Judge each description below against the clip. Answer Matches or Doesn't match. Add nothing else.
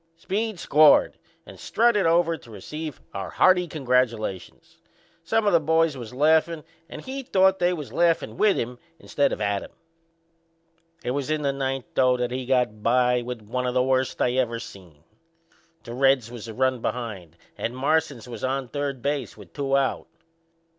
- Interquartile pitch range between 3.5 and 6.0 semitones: Matches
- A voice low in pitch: Matches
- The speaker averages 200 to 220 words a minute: Doesn't match